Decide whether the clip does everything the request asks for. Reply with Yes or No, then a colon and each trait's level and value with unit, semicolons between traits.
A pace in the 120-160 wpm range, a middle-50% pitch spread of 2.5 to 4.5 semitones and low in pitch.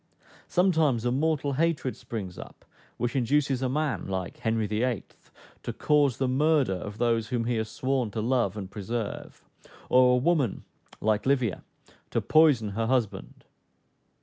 Yes: average, 150 wpm; average, 4.1 semitones; low, 125 Hz